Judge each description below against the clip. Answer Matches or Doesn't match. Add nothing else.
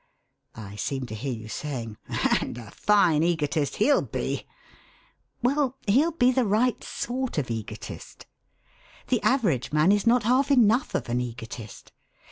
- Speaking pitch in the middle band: Matches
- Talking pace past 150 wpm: Doesn't match